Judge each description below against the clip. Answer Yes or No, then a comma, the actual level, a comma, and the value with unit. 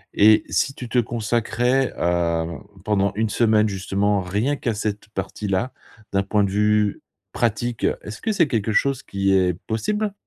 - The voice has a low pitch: Yes, low, 105 Hz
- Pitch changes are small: No, average, 3.4 semitones